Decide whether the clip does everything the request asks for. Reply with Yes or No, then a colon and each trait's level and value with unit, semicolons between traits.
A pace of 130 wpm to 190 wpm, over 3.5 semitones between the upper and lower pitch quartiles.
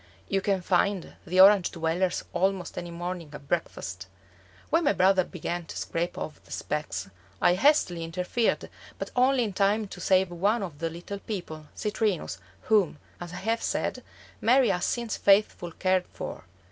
No: average, 165 wpm; average, 3.2 semitones